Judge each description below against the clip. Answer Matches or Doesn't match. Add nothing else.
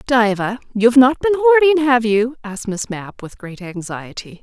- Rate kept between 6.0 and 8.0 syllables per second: Doesn't match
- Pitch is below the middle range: Doesn't match